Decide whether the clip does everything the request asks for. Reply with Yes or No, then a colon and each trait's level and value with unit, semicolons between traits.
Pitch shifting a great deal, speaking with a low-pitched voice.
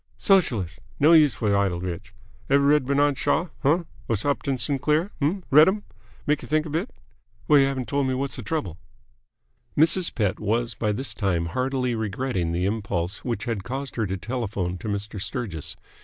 Yes: wide, 6.2 semitones; low, 125 Hz